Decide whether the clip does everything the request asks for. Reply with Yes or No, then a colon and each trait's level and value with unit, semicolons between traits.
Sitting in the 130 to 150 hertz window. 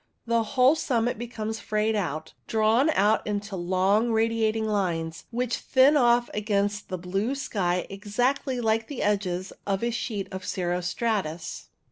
No: high, 215 Hz